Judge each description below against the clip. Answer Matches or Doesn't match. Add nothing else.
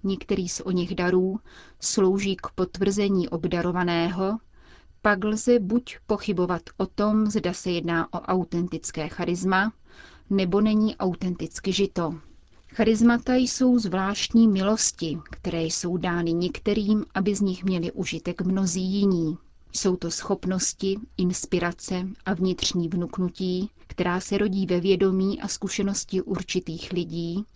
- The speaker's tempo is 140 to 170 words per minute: Doesn't match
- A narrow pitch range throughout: Matches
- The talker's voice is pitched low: Doesn't match